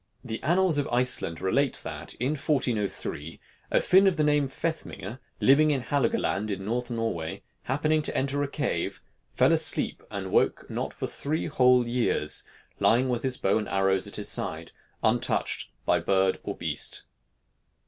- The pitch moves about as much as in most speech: No, wide, 6.4 semitones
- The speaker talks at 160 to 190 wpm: Yes, average, 170 wpm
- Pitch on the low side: Yes, low, 125 Hz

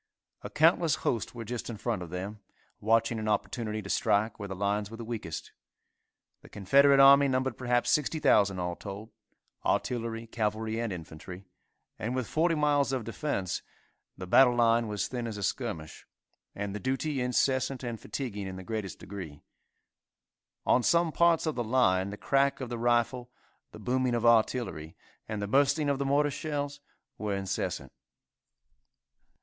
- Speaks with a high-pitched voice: No, low, 115 Hz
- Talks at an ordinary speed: Yes, average, 165 wpm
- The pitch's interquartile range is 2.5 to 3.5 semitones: No, average, 4.7 semitones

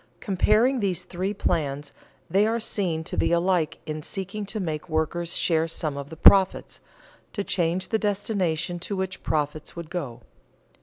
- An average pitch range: Yes, average, 3.9 semitones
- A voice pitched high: No, medium, 175 Hz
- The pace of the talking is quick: No, average, 165 wpm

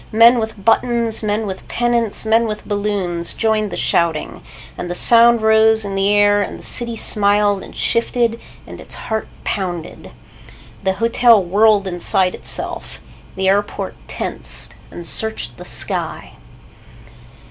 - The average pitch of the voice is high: Yes, high, 210 Hz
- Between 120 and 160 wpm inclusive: Yes, average, 140 wpm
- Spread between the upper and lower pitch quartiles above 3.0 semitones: No, narrow, 2.6 semitones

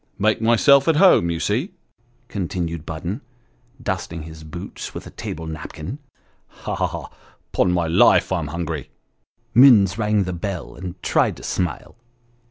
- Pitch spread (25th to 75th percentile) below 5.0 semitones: No, wide, 5.6 semitones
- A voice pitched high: No, very low, 95 Hz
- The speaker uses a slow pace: No, average, 160 wpm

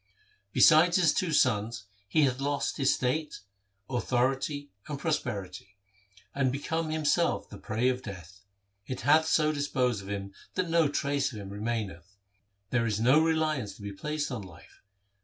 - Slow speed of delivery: No, average, 160 wpm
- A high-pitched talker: No, low, 130 Hz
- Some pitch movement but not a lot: No, wide, 6.2 semitones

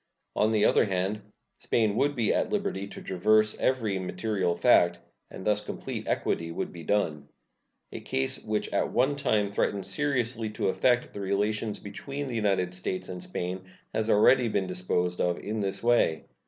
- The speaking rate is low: No, average, 170 wpm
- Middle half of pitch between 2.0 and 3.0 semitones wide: No, average, 3.5 semitones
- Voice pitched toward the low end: Yes, low, 105 Hz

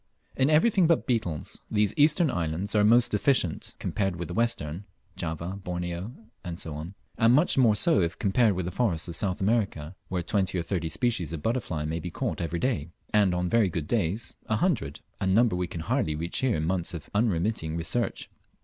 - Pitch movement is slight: No, wide, 5.6 semitones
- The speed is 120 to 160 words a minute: No, average, 195 wpm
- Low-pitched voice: Yes, very low, 95 Hz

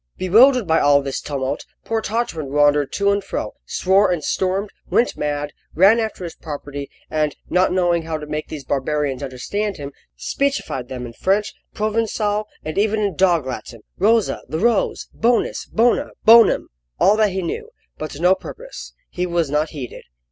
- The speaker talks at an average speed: Yes, average, 170 wpm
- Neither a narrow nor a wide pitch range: No, wide, 6.3 semitones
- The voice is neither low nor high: Yes, medium, 180 Hz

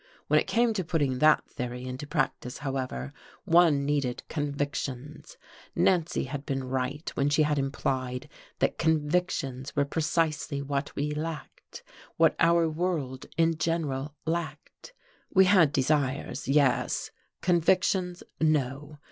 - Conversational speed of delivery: No, slow, 125 wpm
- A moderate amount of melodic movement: Yes, average, 3.3 semitones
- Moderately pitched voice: Yes, medium, 150 Hz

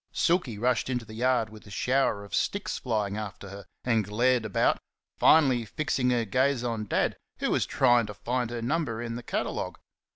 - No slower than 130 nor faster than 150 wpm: No, average, 190 wpm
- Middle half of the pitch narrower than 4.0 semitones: Yes, average, 3.0 semitones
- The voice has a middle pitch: No, low, 120 Hz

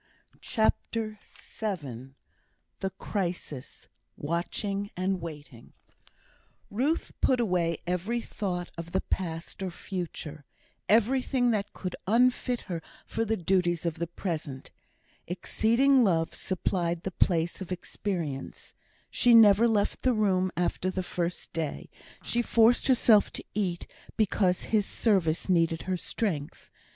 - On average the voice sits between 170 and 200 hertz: Yes, medium, 185 Hz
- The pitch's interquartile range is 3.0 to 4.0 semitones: No, average, 4.4 semitones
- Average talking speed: No, slow, 120 wpm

